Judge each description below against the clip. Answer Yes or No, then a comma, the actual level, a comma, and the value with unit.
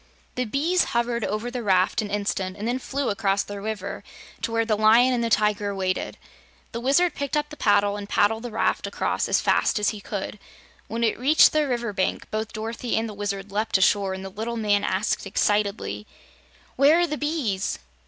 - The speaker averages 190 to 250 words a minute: Yes, fast, 205 wpm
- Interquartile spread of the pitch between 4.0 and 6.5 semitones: No, average, 3.2 semitones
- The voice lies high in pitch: Yes, high, 215 Hz